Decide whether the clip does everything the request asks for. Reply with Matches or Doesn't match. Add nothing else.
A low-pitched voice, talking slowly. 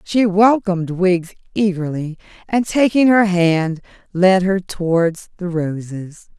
Doesn't match